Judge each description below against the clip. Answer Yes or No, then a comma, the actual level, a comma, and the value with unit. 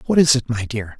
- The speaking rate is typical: No, fast, 300 wpm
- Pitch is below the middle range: Yes, low, 125 Hz